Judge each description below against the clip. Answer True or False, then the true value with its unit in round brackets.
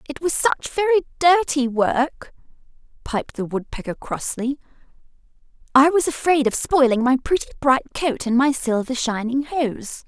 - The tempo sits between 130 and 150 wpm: True (145 wpm)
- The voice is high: True (270 Hz)